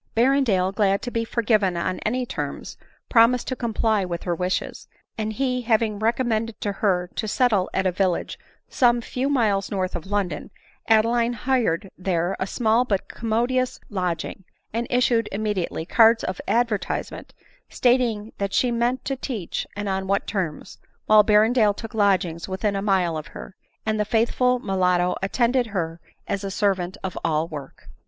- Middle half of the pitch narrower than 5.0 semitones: Yes, average, 3.9 semitones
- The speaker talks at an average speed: Yes, average, 165 wpm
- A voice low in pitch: No, high, 210 Hz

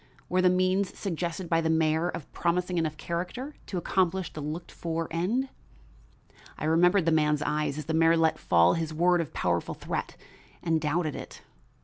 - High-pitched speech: No, medium, 165 Hz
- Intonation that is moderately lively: No, narrow, 2.2 semitones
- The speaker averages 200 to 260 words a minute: No, average, 175 wpm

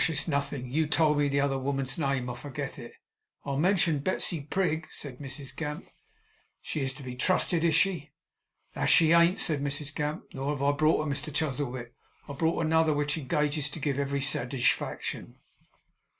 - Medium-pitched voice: Yes, medium, 145 Hz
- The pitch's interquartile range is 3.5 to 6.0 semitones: No, narrow, 2.6 semitones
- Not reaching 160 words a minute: No, average, 180 wpm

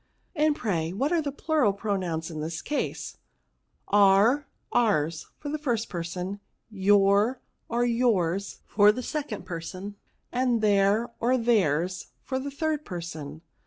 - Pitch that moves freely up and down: Yes, wide, 5.8 semitones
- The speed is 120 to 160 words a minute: Yes, average, 150 wpm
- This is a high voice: Yes, high, 205 Hz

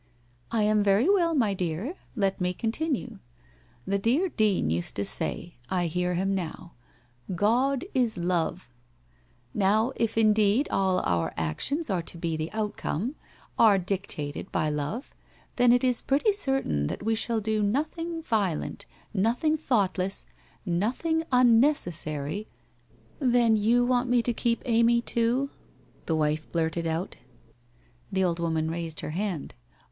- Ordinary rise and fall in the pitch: No, wide, 6.3 semitones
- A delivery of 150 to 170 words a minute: Yes, average, 160 wpm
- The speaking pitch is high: Yes, high, 205 Hz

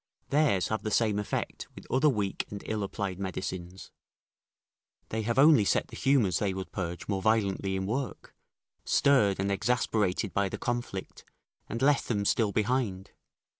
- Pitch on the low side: Yes, low, 105 Hz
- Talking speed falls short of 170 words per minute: Yes, average, 160 wpm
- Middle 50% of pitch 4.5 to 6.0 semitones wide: No, average, 4.0 semitones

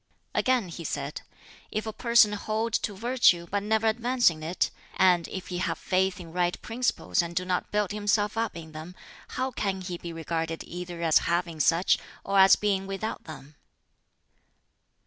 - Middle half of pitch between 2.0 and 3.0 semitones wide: No, average, 4.0 semitones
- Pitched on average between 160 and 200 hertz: Yes, high, 190 Hz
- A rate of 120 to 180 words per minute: Yes, average, 175 wpm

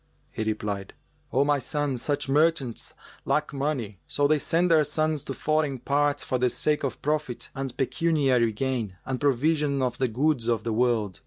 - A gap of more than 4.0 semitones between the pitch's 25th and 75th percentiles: No, average, 3.7 semitones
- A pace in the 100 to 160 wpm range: No, average, 175 wpm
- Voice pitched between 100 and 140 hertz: Yes, low, 135 Hz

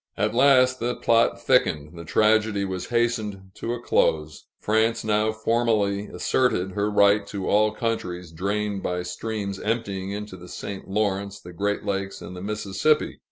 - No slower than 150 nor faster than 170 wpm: Yes, average, 160 wpm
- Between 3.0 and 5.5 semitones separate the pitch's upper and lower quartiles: No, narrow, 2.5 semitones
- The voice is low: Yes, low, 105 Hz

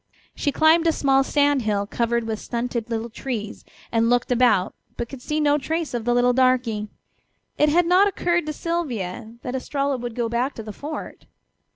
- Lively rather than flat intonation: No, average, 4.2 semitones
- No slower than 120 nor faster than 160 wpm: No, average, 190 wpm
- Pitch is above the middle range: Yes, very high, 250 Hz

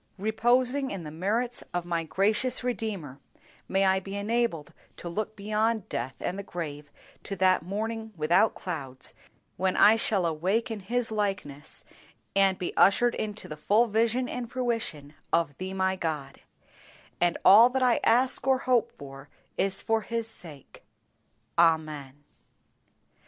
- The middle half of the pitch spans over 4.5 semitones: Yes, wide, 5.4 semitones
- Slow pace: No, average, 145 wpm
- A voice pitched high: Yes, high, 195 Hz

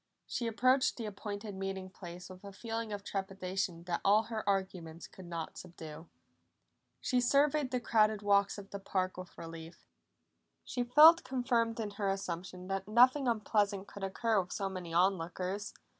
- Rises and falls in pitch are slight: No, average, 3.7 semitones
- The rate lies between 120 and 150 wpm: No, average, 165 wpm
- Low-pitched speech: No, high, 200 Hz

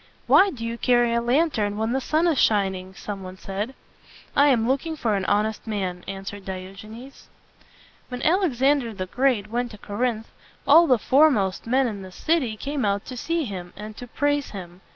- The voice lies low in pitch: No, high, 230 Hz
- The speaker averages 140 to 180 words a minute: No, average, 195 wpm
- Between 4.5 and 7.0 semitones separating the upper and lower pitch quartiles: Yes, average, 5.2 semitones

